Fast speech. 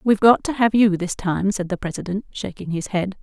Yes: fast, 240 wpm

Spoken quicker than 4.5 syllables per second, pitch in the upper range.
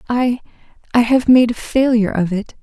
Yes: 5.4 syllables/s; high, 235 Hz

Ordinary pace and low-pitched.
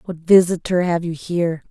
No: average, 175 wpm; medium, 170 Hz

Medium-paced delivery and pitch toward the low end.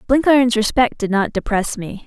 No: average, 175 wpm; high, 230 Hz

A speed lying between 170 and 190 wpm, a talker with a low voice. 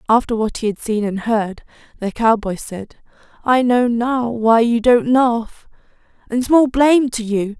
No: average, 175 wpm; high, 230 Hz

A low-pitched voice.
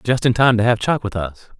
Yes: low, 115 Hz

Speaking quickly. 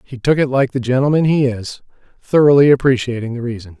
No: average, 190 wpm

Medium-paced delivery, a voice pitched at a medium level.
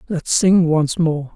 Yes: average, 175 wpm; medium, 170 Hz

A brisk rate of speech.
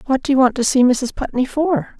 Yes: fast, 300 wpm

